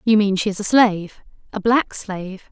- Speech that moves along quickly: No, average, 190 wpm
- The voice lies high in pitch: Yes, high, 205 Hz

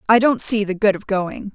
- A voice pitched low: No, high, 205 Hz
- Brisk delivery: Yes, fast, 270 wpm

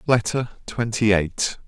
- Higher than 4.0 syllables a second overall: No, 3.8 syllables/s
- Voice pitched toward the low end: Yes, low, 110 Hz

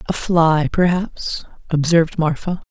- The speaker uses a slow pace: Yes, slow, 110 wpm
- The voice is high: No, medium, 165 Hz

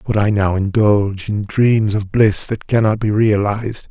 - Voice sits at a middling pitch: No, low, 105 Hz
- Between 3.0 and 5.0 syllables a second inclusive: Yes, 4.5 syllables/s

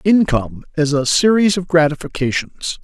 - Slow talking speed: Yes, slow, 125 wpm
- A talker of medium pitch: Yes, medium, 160 Hz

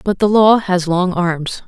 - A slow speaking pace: No, fast, 215 wpm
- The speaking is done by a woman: Yes, female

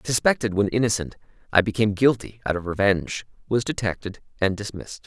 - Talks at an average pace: Yes, average, 155 wpm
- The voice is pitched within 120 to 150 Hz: No, low, 105 Hz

